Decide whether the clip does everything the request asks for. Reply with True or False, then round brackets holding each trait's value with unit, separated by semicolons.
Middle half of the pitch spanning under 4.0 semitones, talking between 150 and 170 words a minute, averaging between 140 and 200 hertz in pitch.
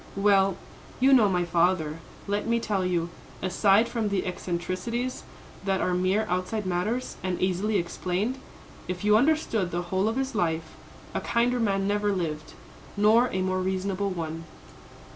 True (3.2 semitones; 155 wpm; 190 Hz)